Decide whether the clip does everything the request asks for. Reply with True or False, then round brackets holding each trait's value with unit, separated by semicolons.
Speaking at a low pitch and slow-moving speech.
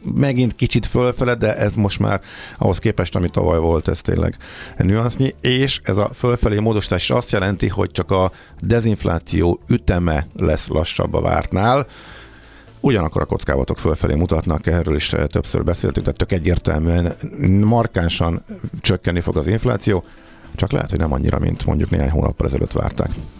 False (95 Hz; 150 wpm)